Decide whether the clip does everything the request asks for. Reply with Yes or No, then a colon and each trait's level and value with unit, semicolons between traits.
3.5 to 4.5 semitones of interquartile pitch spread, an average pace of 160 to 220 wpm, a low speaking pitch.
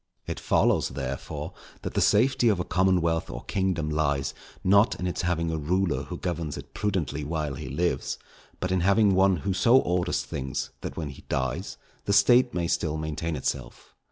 Yes: average, 4.2 semitones; average, 185 wpm; very low, 85 Hz